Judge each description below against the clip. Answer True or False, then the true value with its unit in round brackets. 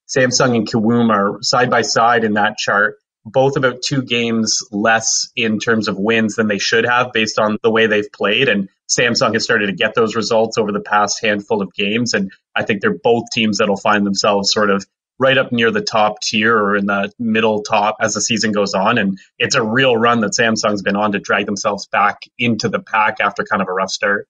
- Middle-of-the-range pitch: False (110 Hz)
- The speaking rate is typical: False (230 wpm)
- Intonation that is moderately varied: False (2.3 semitones)